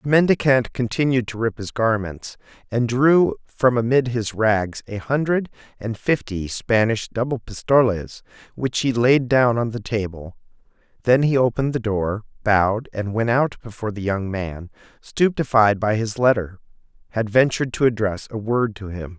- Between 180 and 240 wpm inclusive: No, average, 165 wpm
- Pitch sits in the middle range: No, low, 115 Hz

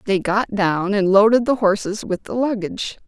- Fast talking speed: No, average, 195 wpm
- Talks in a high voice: Yes, high, 205 Hz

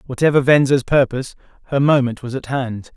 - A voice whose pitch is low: Yes, low, 130 Hz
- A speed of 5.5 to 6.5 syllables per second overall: Yes, 5.8 syllables/s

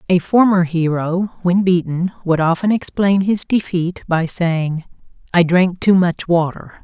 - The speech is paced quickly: No, average, 150 wpm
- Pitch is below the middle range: No, medium, 180 Hz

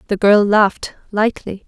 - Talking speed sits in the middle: Yes, average, 145 wpm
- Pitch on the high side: Yes, high, 205 Hz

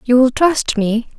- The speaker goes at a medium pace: Yes, average, 150 wpm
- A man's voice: No, female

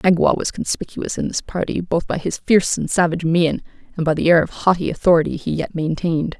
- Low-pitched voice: No, medium, 170 Hz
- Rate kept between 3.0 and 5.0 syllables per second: No, 6.0 syllables/s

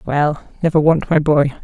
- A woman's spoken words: Yes, female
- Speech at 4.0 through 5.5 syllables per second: Yes, 4.8 syllables/s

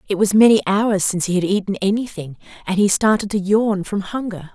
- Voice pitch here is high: Yes, high, 200 Hz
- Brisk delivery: Yes, fast, 210 wpm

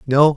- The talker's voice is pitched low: No, medium, 145 Hz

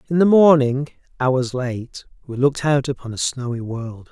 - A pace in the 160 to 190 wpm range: Yes, average, 175 wpm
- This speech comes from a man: Yes, male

